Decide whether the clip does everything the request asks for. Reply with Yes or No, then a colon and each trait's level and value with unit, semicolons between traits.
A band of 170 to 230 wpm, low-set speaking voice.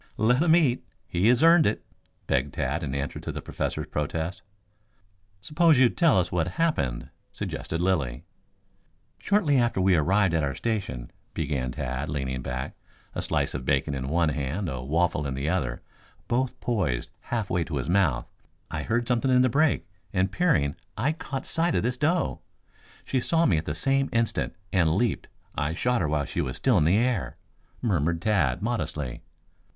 Yes: average, 180 wpm; very low, 90 Hz